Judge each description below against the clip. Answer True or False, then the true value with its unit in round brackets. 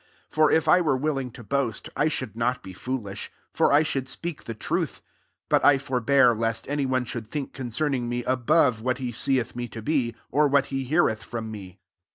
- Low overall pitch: True (130 Hz)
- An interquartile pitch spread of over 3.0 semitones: True (3.5 semitones)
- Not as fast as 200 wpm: False (205 wpm)